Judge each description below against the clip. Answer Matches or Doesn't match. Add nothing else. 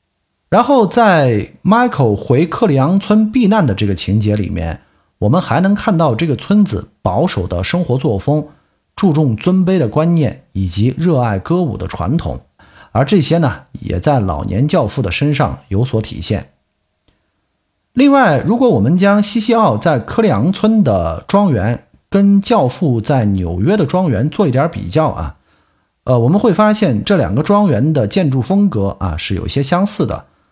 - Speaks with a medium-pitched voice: Matches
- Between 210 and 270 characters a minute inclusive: Matches